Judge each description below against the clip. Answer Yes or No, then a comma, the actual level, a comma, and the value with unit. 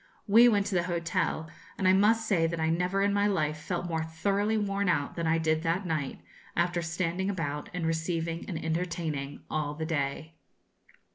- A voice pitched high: No, medium, 170 Hz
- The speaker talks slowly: No, average, 190 wpm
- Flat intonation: No, average, 3.1 semitones